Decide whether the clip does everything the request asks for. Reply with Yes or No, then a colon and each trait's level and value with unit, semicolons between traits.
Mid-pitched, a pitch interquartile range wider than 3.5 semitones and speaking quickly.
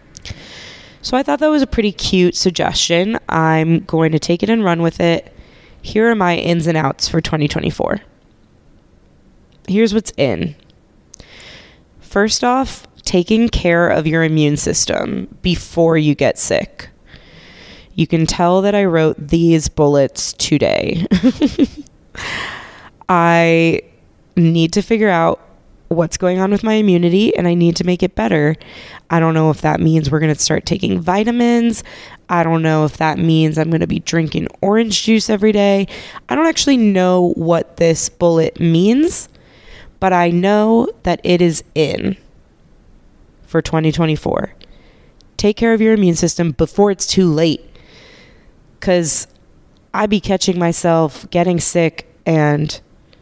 No: medium, 175 Hz; average, 3.9 semitones; average, 145 wpm